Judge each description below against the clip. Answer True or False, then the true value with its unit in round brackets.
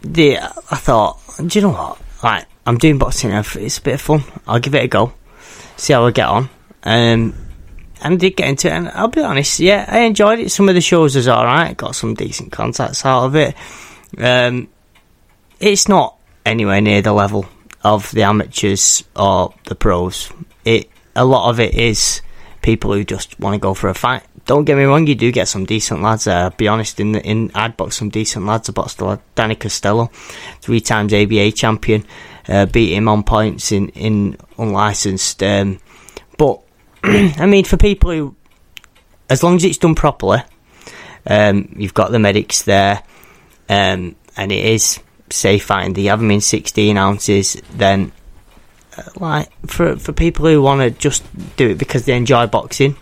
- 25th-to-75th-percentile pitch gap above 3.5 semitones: True (5.4 semitones)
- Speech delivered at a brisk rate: False (190 wpm)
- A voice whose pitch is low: True (110 Hz)